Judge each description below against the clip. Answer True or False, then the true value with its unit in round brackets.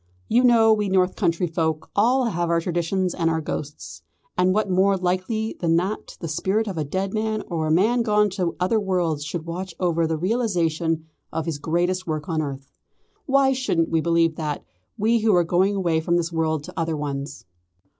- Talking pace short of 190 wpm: False (195 wpm)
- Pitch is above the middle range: False (175 Hz)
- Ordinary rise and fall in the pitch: True (3.8 semitones)